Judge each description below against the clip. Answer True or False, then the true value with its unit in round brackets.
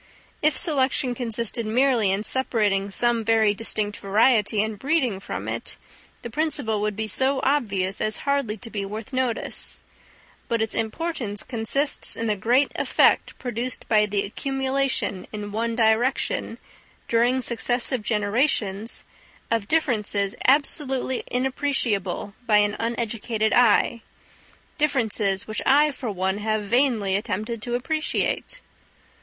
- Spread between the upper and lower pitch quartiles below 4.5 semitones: True (3.9 semitones)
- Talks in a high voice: True (230 Hz)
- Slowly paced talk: True (125 wpm)